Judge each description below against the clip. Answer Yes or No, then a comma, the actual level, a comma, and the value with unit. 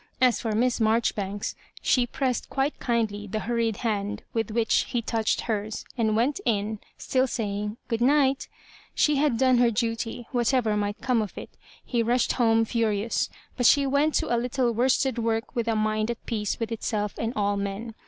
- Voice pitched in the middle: No, high, 230 Hz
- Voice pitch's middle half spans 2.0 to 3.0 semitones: Yes, narrow, 2.4 semitones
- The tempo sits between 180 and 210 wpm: Yes, average, 190 wpm